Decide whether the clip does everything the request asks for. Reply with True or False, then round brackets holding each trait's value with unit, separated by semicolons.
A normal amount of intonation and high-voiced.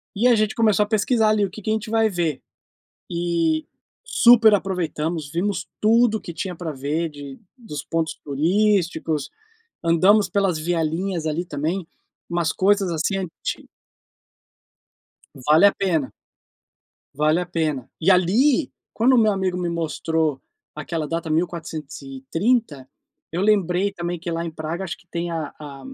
False (4.2 semitones; 175 Hz)